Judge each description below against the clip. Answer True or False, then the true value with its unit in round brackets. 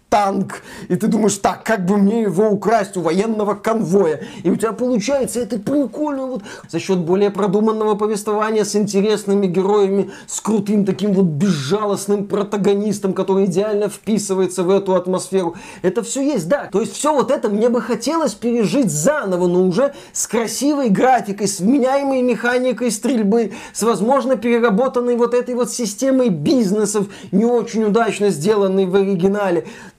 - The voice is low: False (210 Hz)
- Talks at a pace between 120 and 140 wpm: False (155 wpm)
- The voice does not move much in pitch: False (3.4 semitones)